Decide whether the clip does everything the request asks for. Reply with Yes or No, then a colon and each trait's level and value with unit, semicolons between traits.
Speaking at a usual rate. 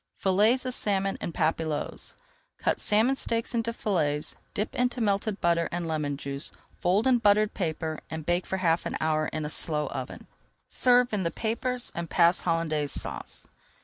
Yes: average, 170 wpm